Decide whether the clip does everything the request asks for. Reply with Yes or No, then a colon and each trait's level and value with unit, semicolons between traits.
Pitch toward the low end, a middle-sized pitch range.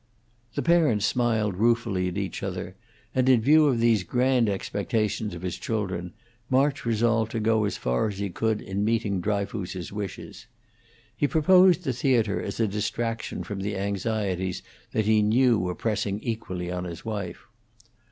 Yes: low, 105 Hz; average, 3.3 semitones